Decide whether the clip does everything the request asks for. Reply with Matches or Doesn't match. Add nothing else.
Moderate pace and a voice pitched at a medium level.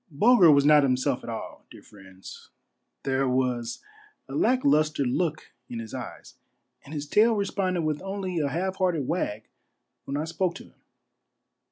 Matches